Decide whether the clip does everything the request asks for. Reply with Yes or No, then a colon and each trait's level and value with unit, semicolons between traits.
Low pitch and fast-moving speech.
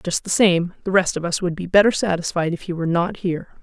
No: medium, 180 Hz; fast, 265 wpm